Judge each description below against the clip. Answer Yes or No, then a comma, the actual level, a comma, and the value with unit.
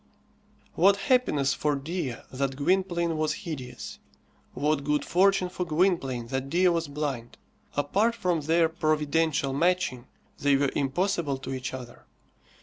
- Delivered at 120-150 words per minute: Yes, slow, 135 wpm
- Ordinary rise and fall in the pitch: Yes, average, 4.5 semitones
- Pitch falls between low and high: Yes, medium, 155 Hz